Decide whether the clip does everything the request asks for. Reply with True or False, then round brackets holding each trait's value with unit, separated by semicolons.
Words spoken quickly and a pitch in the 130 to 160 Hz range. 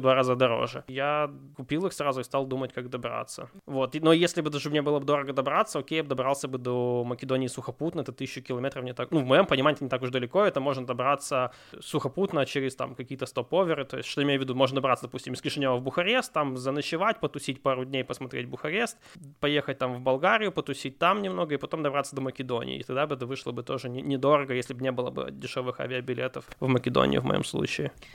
True (225 wpm; 135 Hz)